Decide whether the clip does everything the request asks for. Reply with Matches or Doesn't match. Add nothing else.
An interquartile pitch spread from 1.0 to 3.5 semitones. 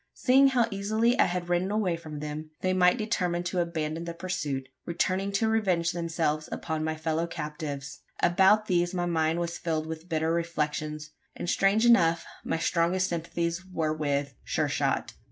Matches